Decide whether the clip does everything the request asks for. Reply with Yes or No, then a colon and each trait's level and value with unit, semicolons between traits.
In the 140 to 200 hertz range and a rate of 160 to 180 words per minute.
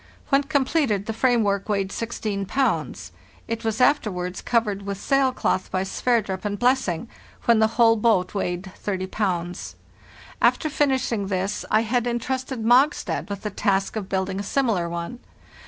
No: high, 215 Hz; average, 165 wpm